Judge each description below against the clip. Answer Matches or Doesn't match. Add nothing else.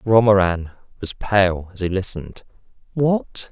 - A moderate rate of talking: Doesn't match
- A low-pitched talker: Matches